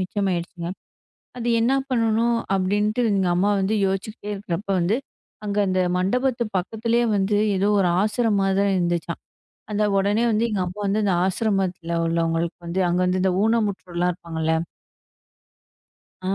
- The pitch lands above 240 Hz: No, high, 195 Hz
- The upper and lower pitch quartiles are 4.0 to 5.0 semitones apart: No, average, 3.1 semitones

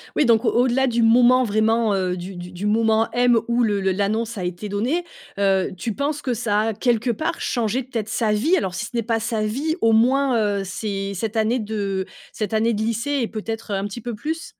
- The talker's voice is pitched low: No, high, 225 Hz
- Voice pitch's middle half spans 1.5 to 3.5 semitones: Yes, average, 2.9 semitones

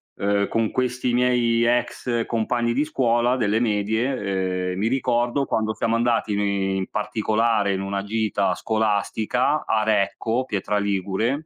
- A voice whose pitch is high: No, low, 110 Hz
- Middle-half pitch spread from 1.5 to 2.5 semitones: No, average, 2.9 semitones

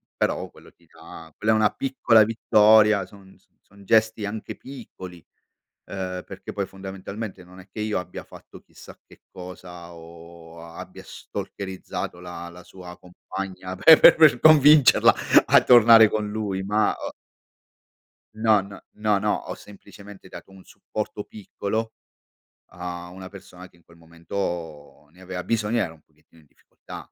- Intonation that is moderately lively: Yes, average, 3.3 semitones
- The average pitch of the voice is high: No, very low, 95 Hz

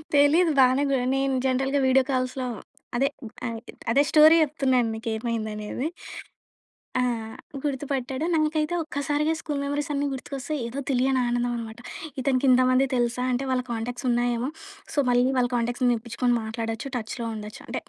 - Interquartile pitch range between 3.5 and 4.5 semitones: No, average, 2.7 semitones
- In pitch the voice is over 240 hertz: Yes, very high, 255 Hz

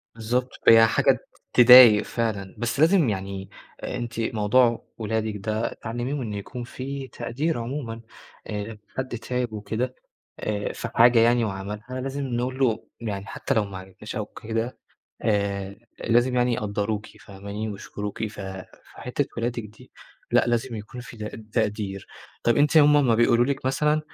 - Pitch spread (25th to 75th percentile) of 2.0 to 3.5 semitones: Yes, average, 3.0 semitones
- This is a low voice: Yes, low, 115 Hz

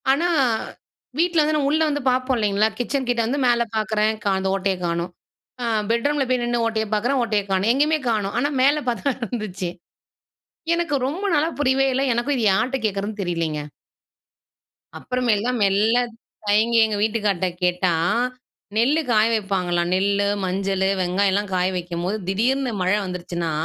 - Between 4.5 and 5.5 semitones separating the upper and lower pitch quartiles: Yes, average, 5.0 semitones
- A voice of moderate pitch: No, high, 220 Hz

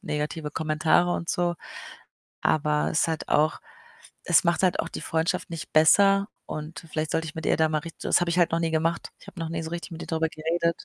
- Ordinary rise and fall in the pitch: No, narrow, 1.6 semitones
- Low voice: No, medium, 165 Hz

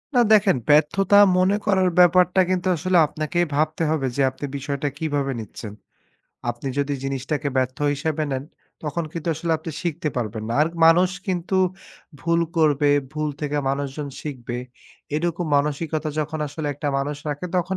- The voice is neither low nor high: Yes, medium, 155 Hz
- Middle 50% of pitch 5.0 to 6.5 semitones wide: No, average, 3.4 semitones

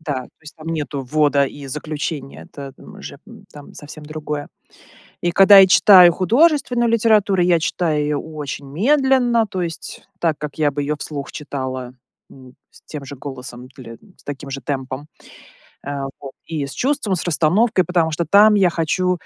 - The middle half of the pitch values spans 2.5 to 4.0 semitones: No, average, 4.7 semitones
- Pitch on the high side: No, medium, 155 Hz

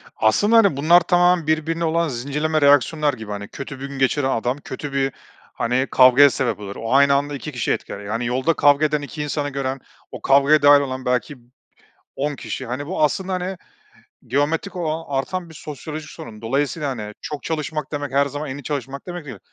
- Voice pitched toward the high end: No, medium, 145 Hz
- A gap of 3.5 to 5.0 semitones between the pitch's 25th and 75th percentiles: No, average, 2.9 semitones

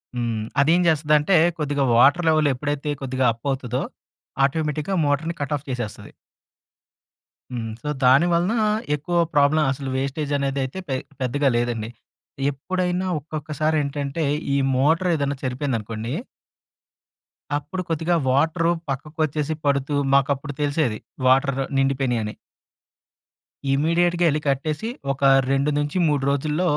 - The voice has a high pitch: No, medium, 145 Hz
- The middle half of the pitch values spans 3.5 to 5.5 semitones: No, average, 2.7 semitones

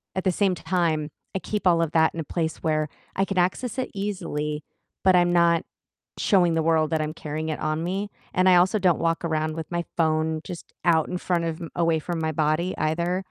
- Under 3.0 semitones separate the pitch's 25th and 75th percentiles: Yes, narrow, 2.5 semitones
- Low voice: No, medium, 165 Hz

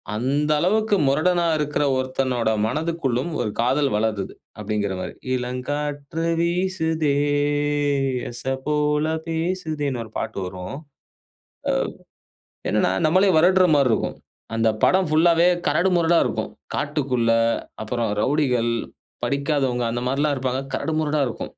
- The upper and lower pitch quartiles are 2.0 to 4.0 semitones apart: No, average, 4.7 semitones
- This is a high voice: No, medium, 145 Hz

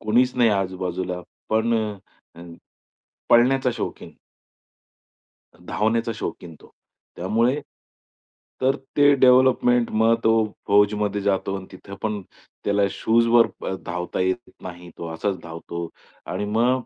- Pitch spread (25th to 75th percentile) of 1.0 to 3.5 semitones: No, average, 4.3 semitones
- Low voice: Yes, low, 105 Hz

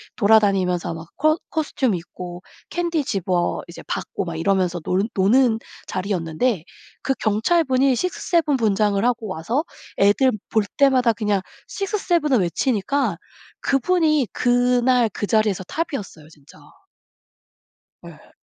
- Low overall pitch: No, high, 220 Hz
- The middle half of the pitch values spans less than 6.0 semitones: No, wide, 6.3 semitones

